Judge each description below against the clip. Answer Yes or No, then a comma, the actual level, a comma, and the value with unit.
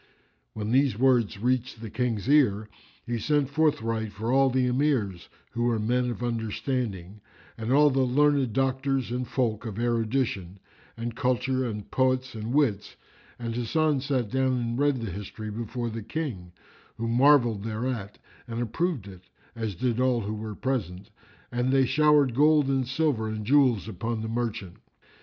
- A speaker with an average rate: Yes, average, 160 wpm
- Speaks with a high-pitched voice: No, low, 120 Hz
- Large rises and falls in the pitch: No, average, 3.3 semitones